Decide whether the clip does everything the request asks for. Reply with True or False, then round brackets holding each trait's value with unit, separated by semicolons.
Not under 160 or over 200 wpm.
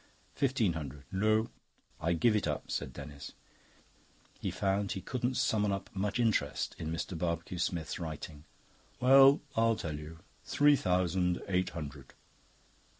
False (140 wpm)